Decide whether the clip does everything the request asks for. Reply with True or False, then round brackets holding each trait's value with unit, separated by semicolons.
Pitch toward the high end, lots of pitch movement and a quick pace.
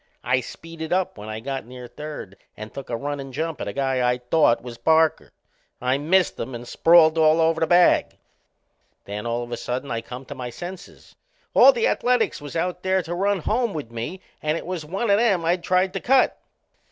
False (155 Hz; 6.3 semitones; 220 wpm)